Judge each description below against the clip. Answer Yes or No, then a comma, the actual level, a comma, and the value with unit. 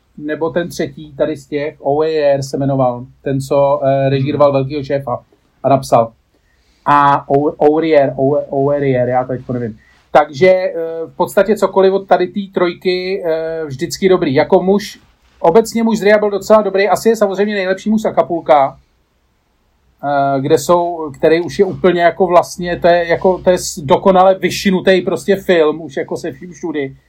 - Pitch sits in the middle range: Yes, medium, 165 Hz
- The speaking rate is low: No, average, 155 wpm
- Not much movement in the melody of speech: No, average, 4.8 semitones